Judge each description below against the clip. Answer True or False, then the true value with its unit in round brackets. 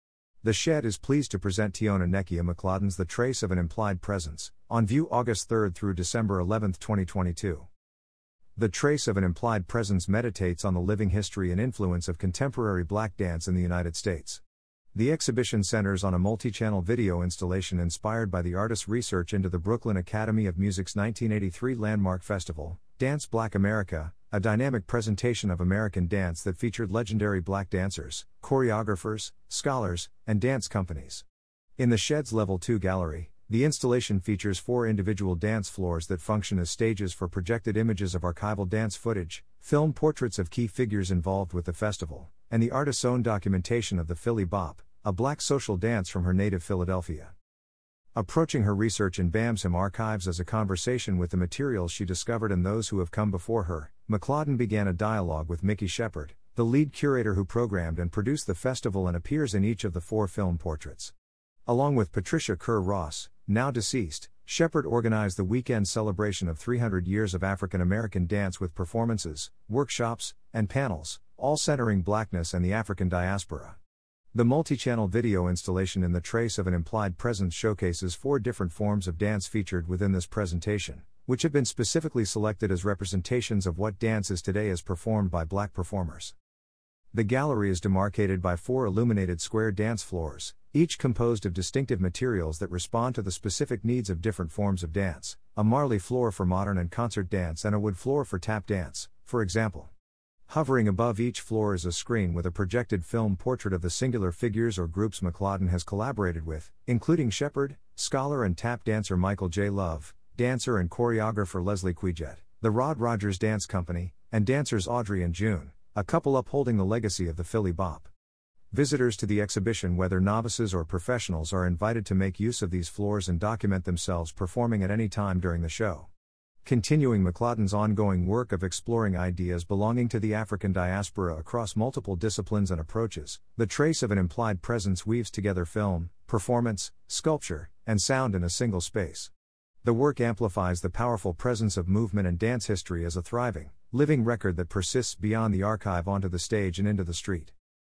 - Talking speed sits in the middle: True (180 wpm)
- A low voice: True (100 Hz)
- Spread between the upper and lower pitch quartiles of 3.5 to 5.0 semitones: True (4.1 semitones)